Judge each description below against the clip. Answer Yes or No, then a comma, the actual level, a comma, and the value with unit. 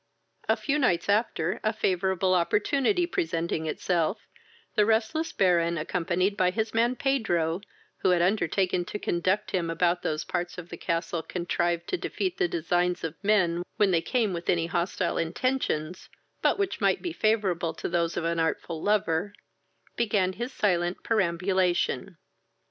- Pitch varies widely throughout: No, average, 4.0 semitones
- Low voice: No, medium, 180 Hz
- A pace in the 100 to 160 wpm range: Yes, average, 155 wpm